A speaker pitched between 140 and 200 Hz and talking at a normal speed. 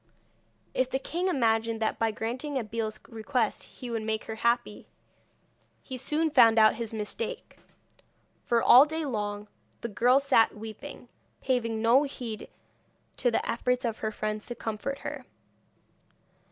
No: high, 230 Hz; average, 145 wpm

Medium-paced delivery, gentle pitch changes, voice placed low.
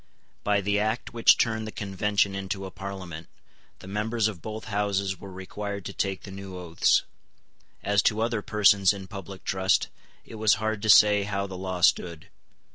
Yes: average, 180 wpm; narrow, 1.9 semitones; low, 100 Hz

